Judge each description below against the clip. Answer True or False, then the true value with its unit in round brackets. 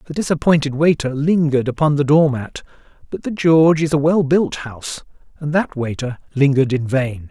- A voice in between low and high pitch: True (145 Hz)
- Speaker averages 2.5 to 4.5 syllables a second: False (5.4 syllables/s)